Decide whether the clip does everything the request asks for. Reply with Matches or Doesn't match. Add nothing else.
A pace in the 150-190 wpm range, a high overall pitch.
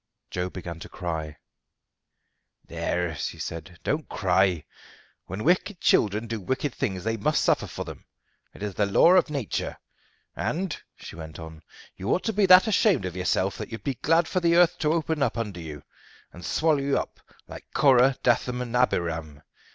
Doesn't match